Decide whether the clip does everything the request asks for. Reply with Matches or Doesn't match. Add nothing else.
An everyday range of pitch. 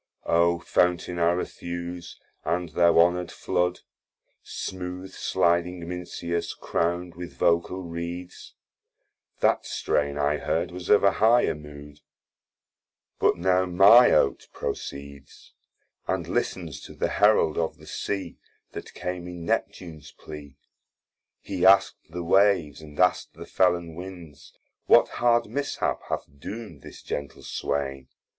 Doesn't match